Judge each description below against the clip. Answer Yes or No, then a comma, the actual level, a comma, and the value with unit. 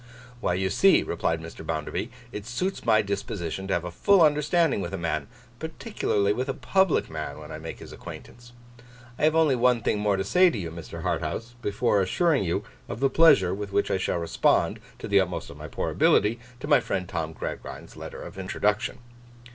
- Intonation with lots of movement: Yes, wide, 6.9 semitones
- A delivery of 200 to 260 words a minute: Yes, fast, 205 wpm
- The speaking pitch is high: No, low, 105 Hz